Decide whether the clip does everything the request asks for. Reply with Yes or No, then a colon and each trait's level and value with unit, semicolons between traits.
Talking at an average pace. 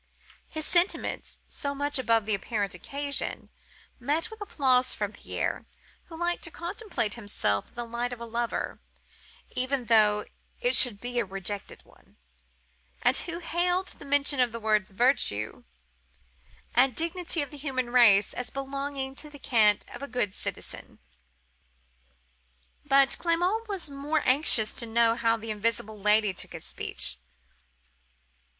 Yes: average, 145 wpm